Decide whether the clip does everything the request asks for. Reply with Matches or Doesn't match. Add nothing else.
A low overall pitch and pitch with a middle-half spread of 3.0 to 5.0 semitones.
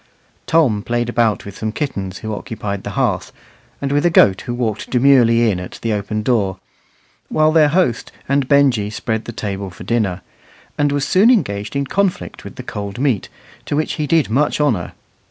Doesn't match